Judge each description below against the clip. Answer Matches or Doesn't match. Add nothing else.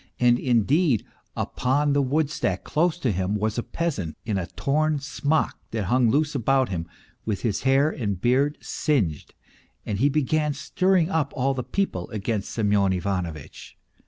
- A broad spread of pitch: Matches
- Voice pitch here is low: Matches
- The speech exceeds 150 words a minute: Matches